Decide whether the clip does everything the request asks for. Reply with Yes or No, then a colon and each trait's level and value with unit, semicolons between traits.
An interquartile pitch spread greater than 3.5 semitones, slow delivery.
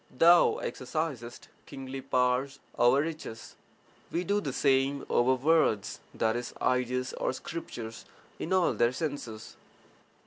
Yes: average, 4.3 semitones; slow, 115 wpm